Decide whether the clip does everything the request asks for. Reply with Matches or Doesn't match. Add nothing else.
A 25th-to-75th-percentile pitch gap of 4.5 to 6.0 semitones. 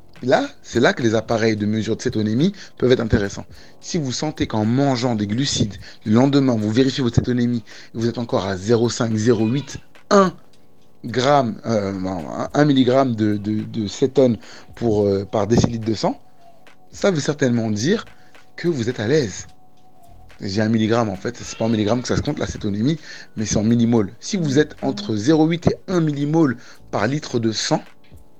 Doesn't match